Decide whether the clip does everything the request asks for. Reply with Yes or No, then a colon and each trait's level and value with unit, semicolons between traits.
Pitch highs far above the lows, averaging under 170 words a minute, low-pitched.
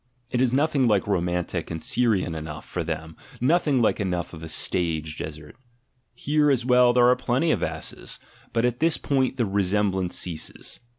No: wide, 6.9 semitones; average, 175 wpm; low, 105 Hz